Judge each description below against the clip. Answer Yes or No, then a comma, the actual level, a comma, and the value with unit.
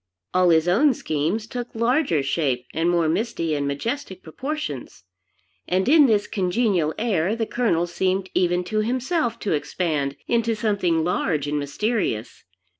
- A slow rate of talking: No, average, 145 wpm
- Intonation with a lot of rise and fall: Yes, wide, 6.3 semitones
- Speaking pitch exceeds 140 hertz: Yes, medium, 185 Hz